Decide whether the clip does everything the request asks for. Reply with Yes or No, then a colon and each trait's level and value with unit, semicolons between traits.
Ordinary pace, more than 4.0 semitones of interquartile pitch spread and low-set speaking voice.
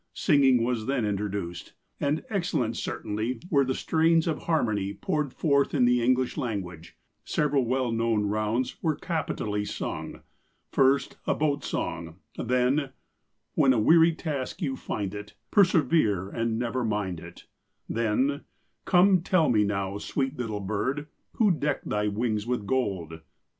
Yes: average, 160 wpm; wide, 5.6 semitones; low, 125 Hz